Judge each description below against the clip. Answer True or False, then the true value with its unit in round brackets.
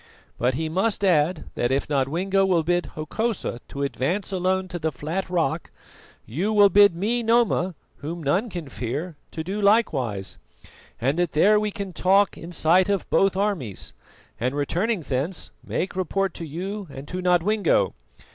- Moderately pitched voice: True (175 Hz)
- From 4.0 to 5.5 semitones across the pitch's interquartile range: True (4.6 semitones)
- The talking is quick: False (165 wpm)